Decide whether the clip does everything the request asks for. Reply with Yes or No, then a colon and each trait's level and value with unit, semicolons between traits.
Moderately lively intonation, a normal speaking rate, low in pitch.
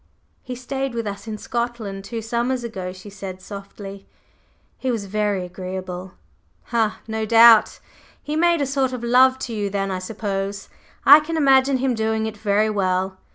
No: average, 4.1 semitones; average, 175 wpm; high, 220 Hz